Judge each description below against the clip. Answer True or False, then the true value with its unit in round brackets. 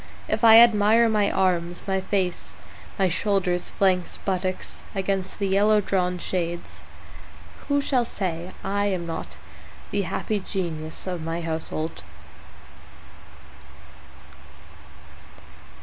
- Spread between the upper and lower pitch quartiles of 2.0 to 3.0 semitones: True (2.6 semitones)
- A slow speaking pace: True (105 wpm)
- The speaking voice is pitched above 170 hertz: True (190 Hz)